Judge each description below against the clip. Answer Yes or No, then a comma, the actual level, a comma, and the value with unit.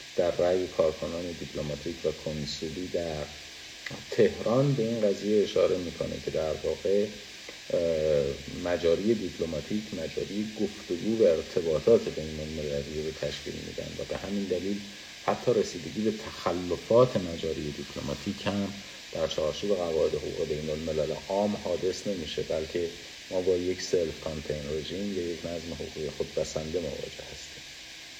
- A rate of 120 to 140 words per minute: Yes, average, 130 wpm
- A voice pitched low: Yes, very low, 90 Hz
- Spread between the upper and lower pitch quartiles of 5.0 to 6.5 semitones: Yes, wide, 5.5 semitones